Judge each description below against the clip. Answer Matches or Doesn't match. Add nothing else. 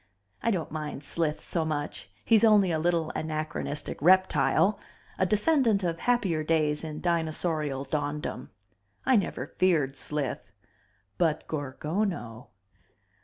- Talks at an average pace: Doesn't match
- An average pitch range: Matches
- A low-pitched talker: Doesn't match